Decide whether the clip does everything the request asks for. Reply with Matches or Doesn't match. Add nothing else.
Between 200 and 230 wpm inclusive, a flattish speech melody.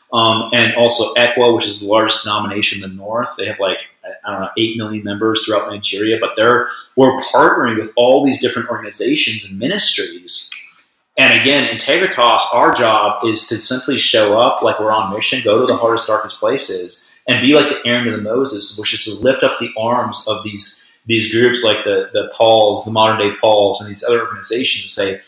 Matches